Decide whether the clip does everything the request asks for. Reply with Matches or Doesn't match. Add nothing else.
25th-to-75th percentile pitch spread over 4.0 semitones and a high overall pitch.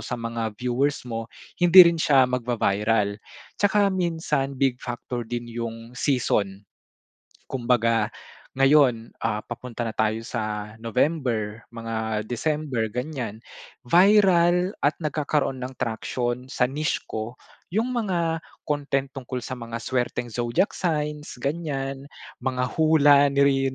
Doesn't match